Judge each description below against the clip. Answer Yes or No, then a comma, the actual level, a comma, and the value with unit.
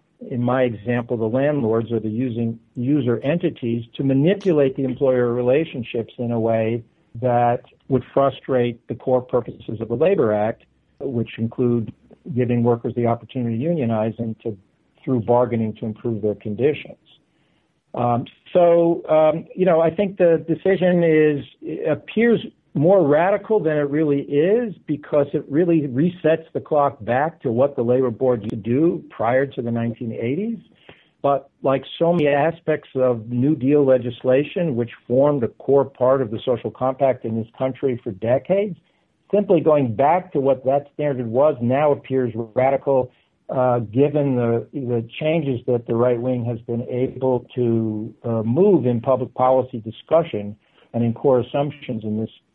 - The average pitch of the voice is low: Yes, low, 130 Hz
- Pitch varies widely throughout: No, average, 4.0 semitones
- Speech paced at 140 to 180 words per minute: Yes, average, 160 wpm